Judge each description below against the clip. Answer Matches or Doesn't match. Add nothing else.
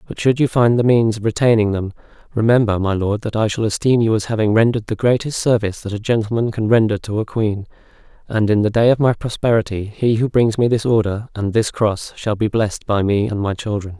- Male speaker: Matches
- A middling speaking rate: Doesn't match